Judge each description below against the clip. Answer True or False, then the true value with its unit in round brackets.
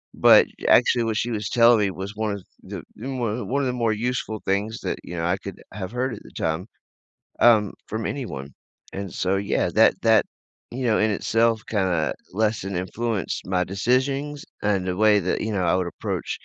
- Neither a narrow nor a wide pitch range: True (3.5 semitones)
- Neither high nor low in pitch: False (105 Hz)